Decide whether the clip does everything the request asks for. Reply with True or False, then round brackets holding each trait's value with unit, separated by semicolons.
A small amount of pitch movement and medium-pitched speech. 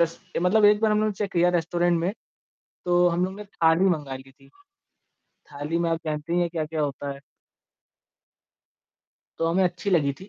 False (3.0 semitones; 170 Hz)